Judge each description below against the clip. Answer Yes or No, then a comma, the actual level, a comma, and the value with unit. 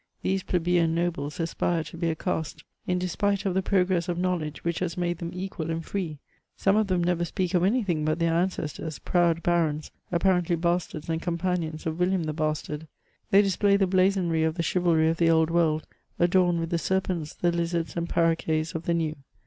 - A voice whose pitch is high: No, medium, 170 Hz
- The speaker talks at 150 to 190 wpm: No, fast, 205 wpm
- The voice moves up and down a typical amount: No, narrow, 2.0 semitones